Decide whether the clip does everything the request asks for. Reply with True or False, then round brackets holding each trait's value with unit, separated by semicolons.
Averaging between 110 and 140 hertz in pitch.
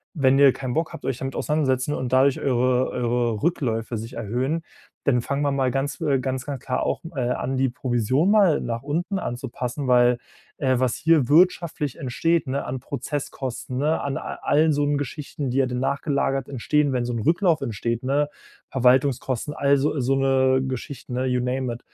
True (135 Hz)